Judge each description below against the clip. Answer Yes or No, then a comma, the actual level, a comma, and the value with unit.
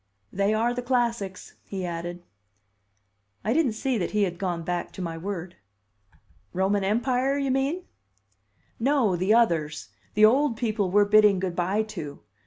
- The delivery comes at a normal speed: Yes, average, 155 wpm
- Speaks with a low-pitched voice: No, high, 205 Hz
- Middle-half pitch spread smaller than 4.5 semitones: No, average, 4.9 semitones